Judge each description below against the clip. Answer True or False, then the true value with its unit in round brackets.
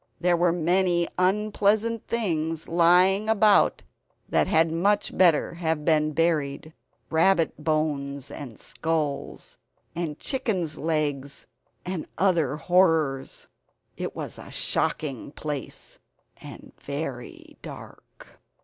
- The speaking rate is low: True (105 wpm)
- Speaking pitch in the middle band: True (165 Hz)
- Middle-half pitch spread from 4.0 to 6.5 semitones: False (3.4 semitones)